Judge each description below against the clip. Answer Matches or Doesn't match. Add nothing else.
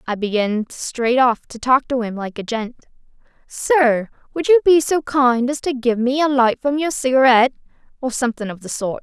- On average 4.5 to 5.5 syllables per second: Matches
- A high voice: Matches